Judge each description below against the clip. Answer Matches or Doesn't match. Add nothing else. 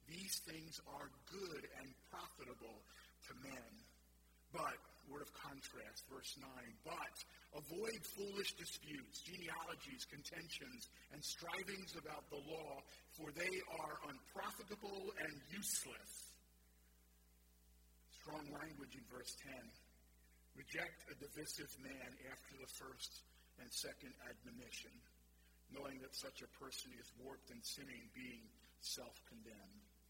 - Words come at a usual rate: Doesn't match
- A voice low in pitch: Doesn't match